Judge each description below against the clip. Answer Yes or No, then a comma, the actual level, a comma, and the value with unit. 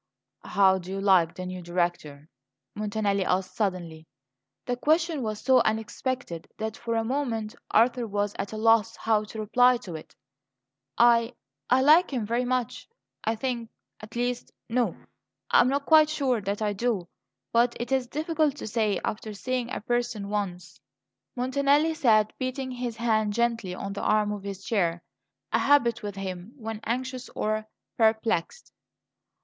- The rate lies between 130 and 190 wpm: Yes, average, 160 wpm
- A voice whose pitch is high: Yes, high, 225 Hz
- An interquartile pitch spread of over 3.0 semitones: Yes, average, 3.7 semitones